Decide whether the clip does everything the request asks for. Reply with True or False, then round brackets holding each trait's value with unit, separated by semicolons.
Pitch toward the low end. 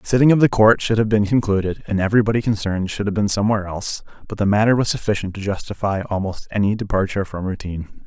True (100 Hz)